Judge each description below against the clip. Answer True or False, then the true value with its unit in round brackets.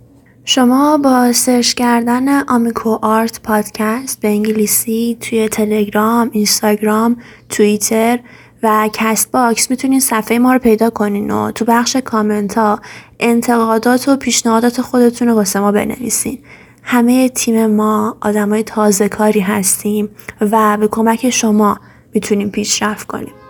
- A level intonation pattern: True (2.1 semitones)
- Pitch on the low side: False (225 Hz)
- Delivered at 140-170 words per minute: False (125 wpm)